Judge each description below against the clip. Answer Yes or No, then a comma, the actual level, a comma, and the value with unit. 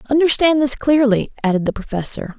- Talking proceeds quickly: No, average, 150 wpm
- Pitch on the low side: No, very high, 255 Hz